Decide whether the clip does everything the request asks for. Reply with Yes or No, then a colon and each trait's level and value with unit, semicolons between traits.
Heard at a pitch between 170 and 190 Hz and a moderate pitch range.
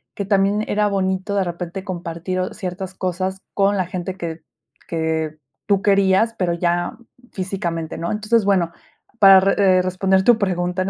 No: medium, 185 Hz; narrow, 2.1 semitones